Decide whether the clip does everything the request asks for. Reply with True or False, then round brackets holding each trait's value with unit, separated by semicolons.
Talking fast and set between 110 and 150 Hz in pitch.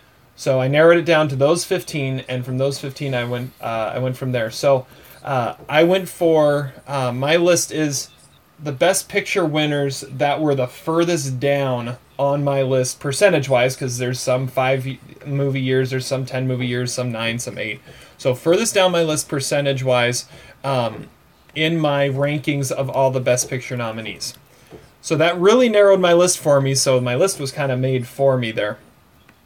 False (185 wpm; 135 Hz)